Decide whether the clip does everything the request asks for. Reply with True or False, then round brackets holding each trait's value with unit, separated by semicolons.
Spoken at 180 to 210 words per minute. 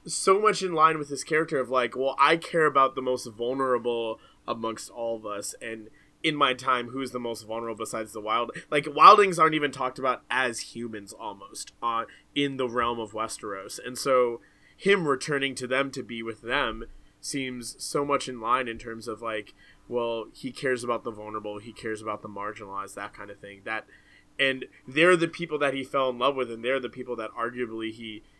True (205 wpm)